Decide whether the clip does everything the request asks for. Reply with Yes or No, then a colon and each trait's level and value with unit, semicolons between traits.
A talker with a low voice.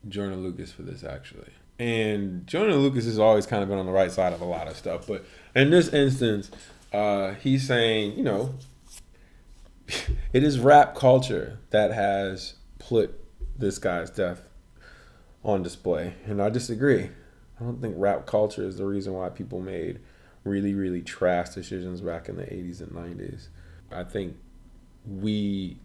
Yes: low, 100 Hz